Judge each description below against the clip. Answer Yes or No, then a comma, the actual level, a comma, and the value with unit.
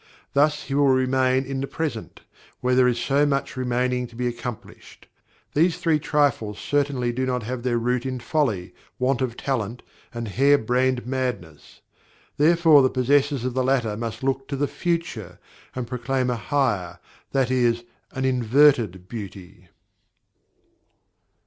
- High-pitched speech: No, low, 130 Hz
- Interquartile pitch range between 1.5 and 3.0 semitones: Yes, narrow, 2.6 semitones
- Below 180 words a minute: Yes, average, 150 wpm